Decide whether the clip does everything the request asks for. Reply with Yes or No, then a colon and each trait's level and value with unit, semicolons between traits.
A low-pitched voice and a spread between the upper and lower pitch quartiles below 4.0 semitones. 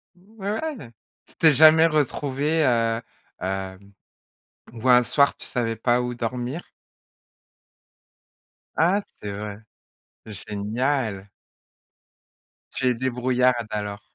No: low, 125 Hz; average, 5.2 semitones